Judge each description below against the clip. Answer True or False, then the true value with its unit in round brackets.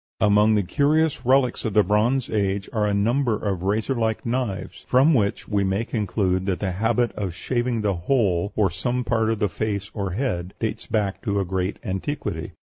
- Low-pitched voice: True (105 Hz)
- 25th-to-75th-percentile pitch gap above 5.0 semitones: False (3.4 semitones)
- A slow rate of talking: False (190 wpm)